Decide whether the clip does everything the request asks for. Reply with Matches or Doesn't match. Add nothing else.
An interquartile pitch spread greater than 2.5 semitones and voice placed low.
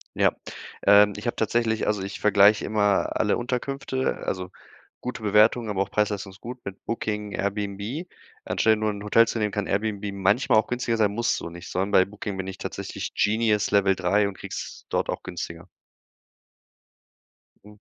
Doesn't match